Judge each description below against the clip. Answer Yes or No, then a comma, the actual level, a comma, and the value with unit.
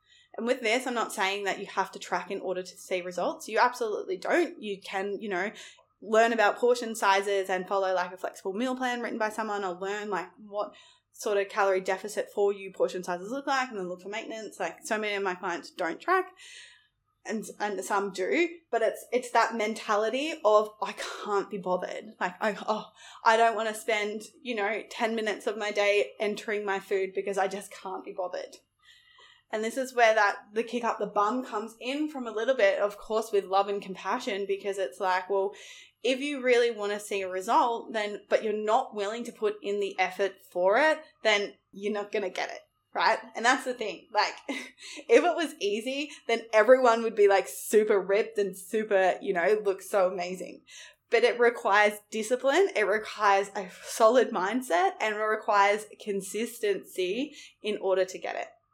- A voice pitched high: Yes, high, 210 Hz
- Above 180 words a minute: Yes, average, 200 wpm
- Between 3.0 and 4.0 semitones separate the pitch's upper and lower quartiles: Yes, average, 3.3 semitones